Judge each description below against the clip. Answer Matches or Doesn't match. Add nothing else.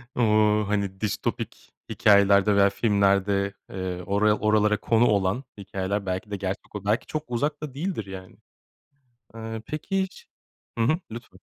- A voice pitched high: Doesn't match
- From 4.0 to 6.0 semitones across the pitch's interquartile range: Doesn't match